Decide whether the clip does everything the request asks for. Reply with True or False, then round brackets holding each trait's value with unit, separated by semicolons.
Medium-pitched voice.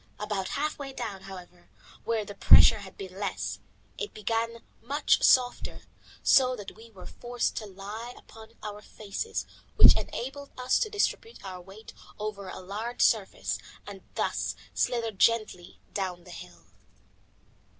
False (215 Hz)